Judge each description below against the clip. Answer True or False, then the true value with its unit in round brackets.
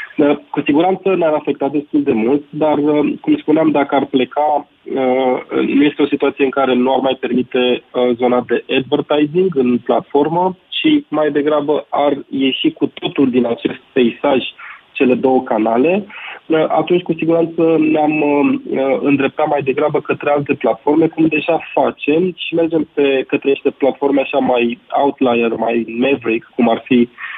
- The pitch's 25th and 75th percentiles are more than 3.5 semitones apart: False (3.0 semitones)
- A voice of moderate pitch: True (145 Hz)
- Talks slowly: False (150 wpm)